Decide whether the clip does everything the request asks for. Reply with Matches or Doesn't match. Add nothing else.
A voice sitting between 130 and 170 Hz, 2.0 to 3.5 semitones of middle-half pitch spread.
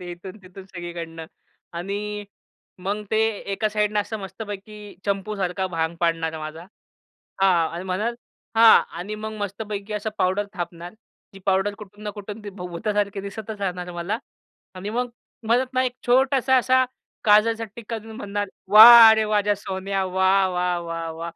Doesn't match